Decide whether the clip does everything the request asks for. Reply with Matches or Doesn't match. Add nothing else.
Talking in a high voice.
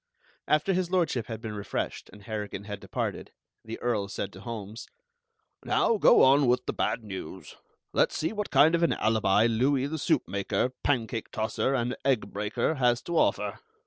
Doesn't match